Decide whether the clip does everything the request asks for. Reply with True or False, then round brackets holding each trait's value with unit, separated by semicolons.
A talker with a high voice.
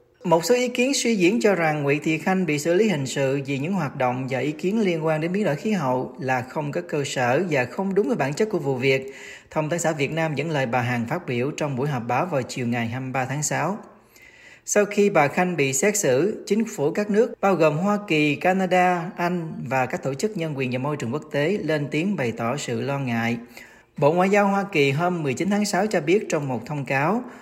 False (155 Hz)